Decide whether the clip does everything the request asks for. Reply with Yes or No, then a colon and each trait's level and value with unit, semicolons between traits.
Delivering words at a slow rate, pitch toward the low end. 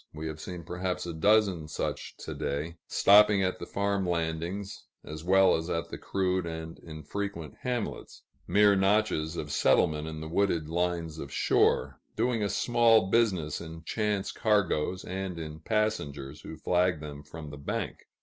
No: average, 160 wpm; very low, 90 Hz